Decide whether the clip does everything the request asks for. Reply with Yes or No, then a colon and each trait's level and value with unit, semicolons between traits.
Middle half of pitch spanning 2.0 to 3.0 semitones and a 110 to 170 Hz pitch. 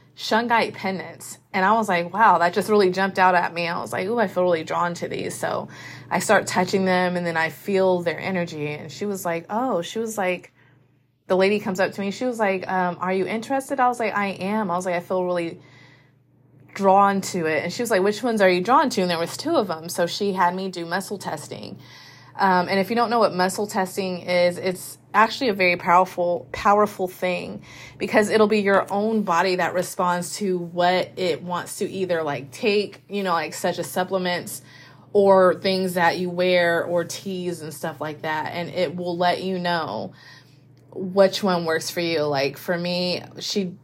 No: narrow, 2.6 semitones; medium, 180 Hz